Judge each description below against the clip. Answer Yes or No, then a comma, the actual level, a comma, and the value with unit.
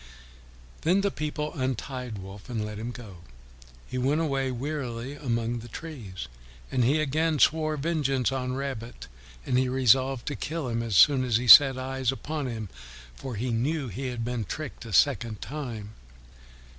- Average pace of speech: Yes, average, 170 wpm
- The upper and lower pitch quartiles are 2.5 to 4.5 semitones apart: Yes, average, 3.7 semitones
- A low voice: Yes, low, 130 Hz